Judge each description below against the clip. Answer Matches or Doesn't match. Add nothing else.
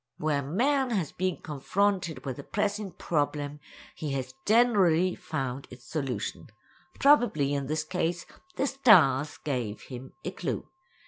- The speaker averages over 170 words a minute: Doesn't match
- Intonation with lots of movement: Matches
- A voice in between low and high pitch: Matches